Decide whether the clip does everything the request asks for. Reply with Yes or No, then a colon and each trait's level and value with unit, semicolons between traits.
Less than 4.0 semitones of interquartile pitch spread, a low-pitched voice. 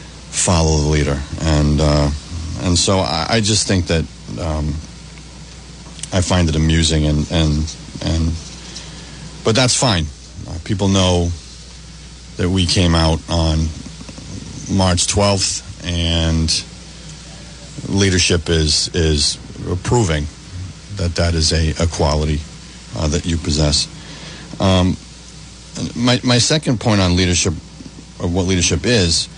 Yes: average, 3.4 semitones; very low, 85 Hz